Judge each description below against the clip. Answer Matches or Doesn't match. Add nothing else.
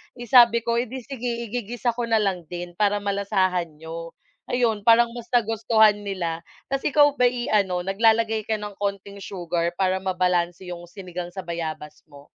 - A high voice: Matches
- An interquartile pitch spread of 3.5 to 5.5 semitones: Matches